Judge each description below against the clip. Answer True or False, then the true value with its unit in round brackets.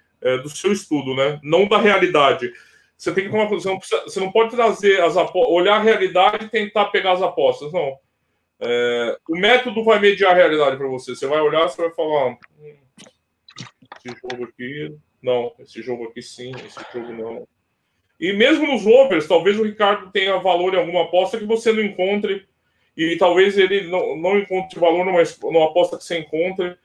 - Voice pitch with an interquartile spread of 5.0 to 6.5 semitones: True (5.5 semitones)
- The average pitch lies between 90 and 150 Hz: False (185 Hz)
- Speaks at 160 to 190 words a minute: True (185 wpm)